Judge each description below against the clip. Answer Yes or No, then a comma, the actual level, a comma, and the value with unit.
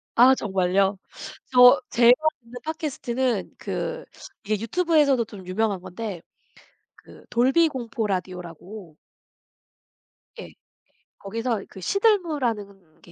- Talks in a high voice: Yes, high, 230 Hz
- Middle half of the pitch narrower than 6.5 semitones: Yes, average, 5.3 semitones